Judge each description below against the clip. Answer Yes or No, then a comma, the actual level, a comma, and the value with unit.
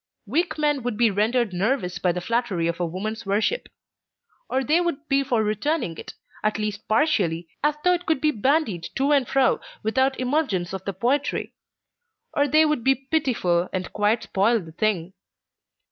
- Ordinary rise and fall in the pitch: No, wide, 6.6 semitones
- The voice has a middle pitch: No, high, 235 Hz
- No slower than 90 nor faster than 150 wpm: No, average, 175 wpm